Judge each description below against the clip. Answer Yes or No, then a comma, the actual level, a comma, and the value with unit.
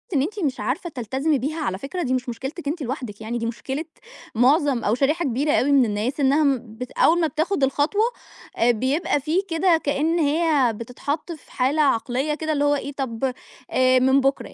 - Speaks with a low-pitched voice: No, very high, 275 Hz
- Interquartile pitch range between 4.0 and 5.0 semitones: No, average, 3.6 semitones